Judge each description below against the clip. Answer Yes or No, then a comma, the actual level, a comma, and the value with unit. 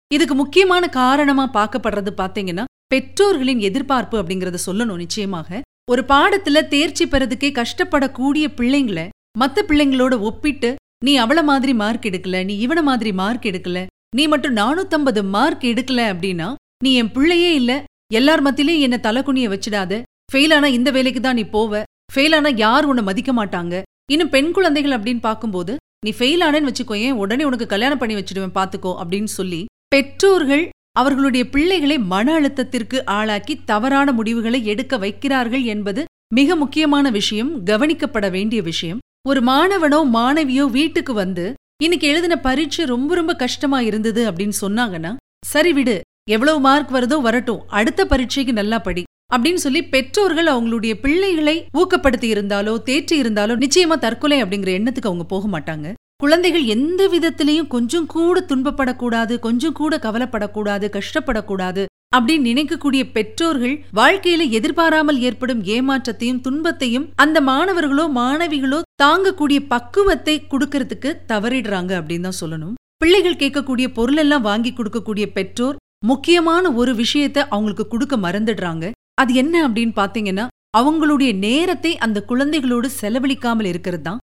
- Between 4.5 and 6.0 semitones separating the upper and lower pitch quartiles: Yes, average, 5.2 semitones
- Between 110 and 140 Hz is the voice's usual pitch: No, very high, 260 Hz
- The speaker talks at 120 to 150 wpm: Yes, fast, 130 wpm